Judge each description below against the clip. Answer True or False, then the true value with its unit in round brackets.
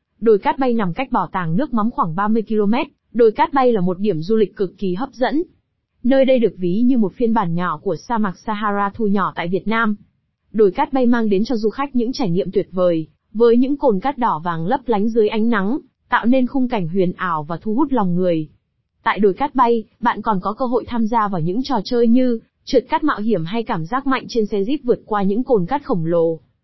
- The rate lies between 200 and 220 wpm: False (250 wpm)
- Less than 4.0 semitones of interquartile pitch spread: False (4.4 semitones)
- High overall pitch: True (220 Hz)